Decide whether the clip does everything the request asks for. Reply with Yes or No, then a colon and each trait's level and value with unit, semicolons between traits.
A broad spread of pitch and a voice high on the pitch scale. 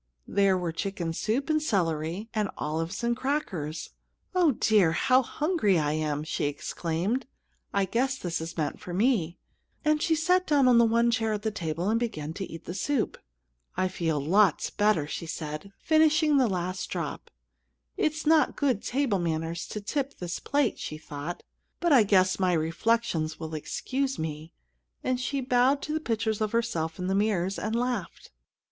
Yes: wide, 7.4 semitones; high, 205 Hz